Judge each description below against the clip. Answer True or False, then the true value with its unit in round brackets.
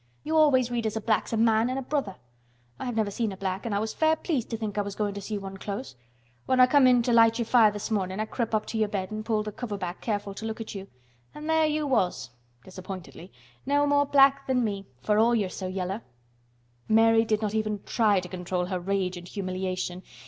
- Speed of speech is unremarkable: False (240 wpm)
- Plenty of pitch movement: False (3.7 semitones)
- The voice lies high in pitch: True (215 Hz)